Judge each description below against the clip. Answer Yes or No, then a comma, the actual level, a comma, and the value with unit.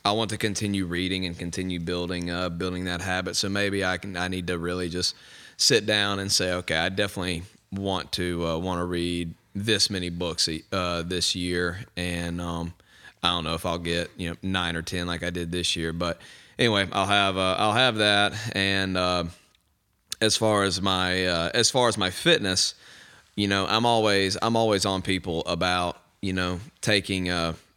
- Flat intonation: Yes, narrow, 2.2 semitones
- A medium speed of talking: Yes, average, 195 wpm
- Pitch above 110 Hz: No, very low, 90 Hz